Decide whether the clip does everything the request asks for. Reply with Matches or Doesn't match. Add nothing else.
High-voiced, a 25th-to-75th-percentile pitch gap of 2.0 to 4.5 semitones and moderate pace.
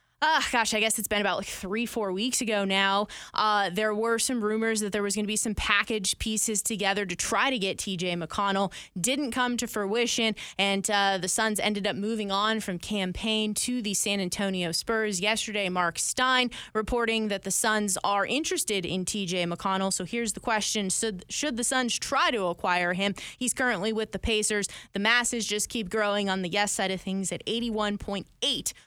Matches